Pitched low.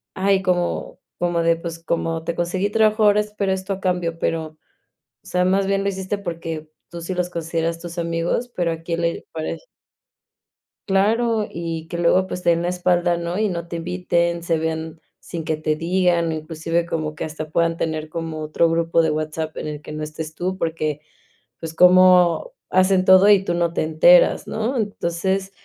No: medium, 170 Hz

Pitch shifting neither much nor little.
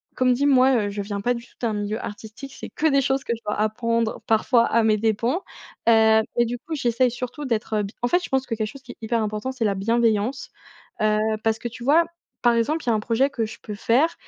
Yes: average, 3.0 semitones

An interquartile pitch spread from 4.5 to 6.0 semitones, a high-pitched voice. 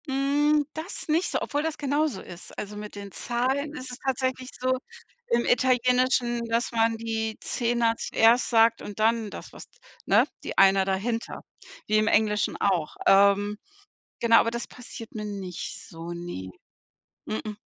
No: average, 3.6 semitones; high, 230 Hz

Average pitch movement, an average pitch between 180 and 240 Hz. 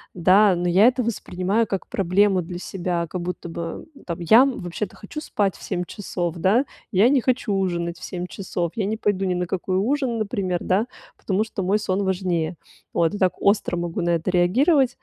Yes: average, 3.2 semitones; high, 190 Hz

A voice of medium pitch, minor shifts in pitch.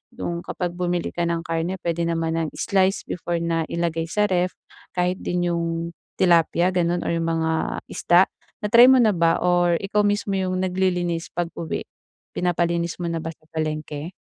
Yes: medium, 175 Hz; narrow, 1.5 semitones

